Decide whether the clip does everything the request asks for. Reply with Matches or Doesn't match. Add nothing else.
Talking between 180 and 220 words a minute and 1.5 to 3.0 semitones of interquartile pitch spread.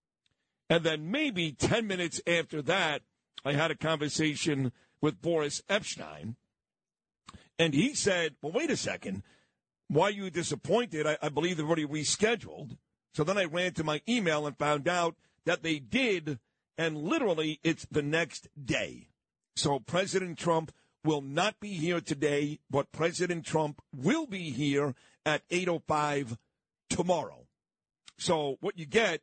Doesn't match